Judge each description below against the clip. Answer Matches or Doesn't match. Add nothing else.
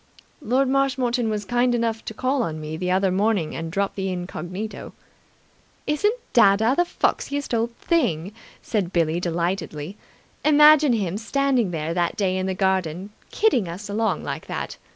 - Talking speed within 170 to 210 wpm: Doesn't match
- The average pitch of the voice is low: Doesn't match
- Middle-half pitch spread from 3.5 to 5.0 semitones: Doesn't match